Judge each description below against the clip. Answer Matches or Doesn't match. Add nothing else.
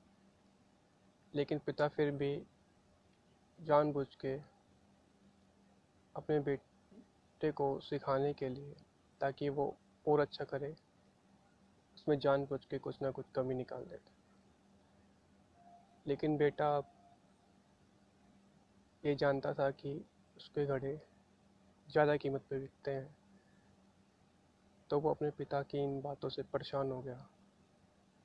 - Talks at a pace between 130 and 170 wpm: Doesn't match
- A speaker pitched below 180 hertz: Matches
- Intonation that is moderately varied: Doesn't match